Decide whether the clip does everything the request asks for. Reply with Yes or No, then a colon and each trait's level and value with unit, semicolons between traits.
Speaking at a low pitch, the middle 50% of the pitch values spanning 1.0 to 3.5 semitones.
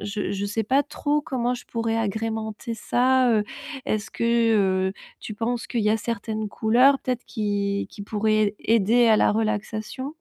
No: high, 220 Hz; narrow, 2.4 semitones